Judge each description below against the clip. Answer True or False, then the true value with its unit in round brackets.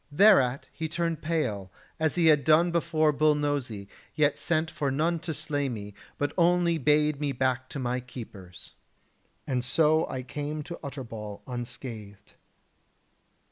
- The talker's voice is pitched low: False (145 Hz)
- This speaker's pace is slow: False (145 wpm)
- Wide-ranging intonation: False (4.1 semitones)